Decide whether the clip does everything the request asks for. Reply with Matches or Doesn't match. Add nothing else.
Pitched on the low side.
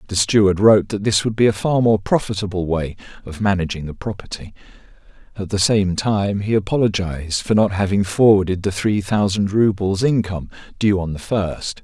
Matches